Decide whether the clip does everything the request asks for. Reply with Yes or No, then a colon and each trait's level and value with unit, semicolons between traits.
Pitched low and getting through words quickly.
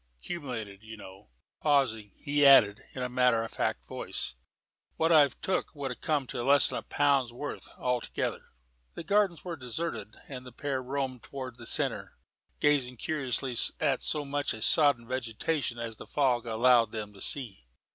No: low, 130 Hz; average, 165 wpm